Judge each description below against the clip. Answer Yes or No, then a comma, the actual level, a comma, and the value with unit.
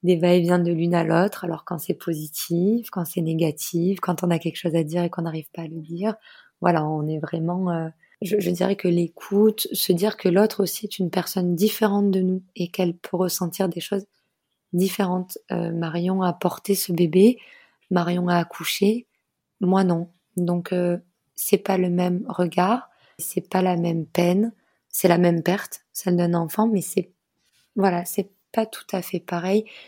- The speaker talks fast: No, average, 190 wpm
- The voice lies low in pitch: No, medium, 180 Hz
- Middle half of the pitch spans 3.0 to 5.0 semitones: No, narrow, 2.5 semitones